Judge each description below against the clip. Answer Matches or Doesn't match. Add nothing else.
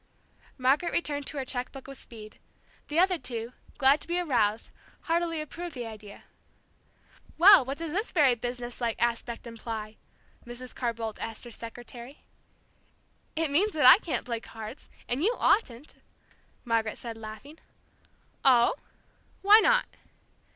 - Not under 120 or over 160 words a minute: Matches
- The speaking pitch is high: Matches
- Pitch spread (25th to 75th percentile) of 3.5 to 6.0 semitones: Matches